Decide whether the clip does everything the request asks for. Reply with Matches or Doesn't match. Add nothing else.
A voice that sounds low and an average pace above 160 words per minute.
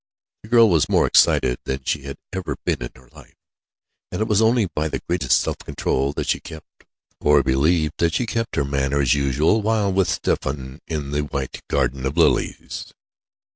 Matches